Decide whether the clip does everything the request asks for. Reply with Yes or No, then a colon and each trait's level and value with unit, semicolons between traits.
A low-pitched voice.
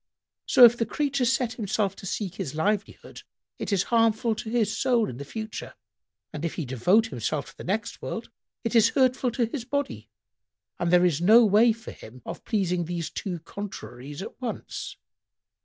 No: high, 210 Hz